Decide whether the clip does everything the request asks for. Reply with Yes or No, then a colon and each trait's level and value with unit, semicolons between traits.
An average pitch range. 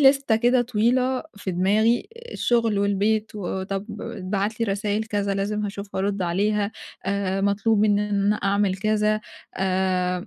No: narrow, 1.8 semitones